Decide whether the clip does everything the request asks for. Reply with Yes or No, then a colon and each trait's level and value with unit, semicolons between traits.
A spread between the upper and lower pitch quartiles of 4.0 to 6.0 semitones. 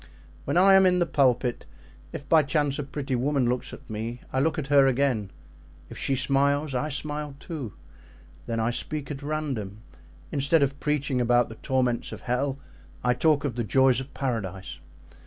No: average, 3.1 semitones